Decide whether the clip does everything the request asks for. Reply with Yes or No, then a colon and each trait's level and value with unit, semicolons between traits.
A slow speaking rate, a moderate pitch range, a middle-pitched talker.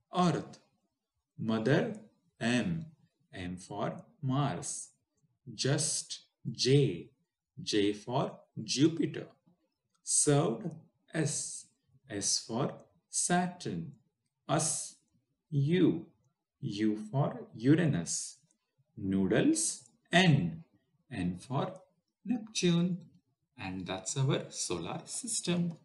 No: slow, 70 wpm; wide, 5.9 semitones; medium, 145 Hz